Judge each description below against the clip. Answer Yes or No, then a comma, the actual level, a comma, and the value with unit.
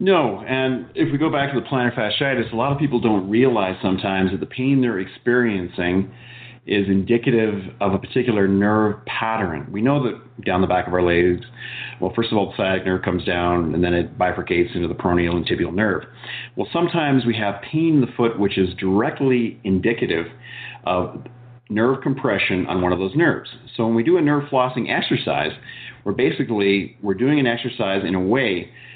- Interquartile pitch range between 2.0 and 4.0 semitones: No, average, 4.8 semitones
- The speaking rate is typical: Yes, average, 195 wpm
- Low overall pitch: Yes, low, 110 Hz